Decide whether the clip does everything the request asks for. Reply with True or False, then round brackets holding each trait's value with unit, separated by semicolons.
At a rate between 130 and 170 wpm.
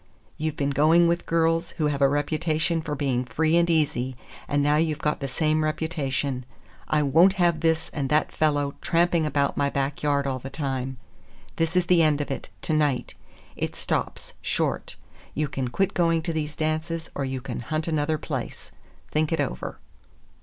False (185 wpm)